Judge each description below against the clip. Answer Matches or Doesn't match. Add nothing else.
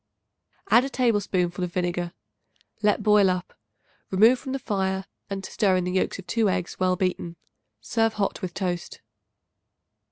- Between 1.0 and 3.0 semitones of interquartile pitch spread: Matches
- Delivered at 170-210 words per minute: Doesn't match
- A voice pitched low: Doesn't match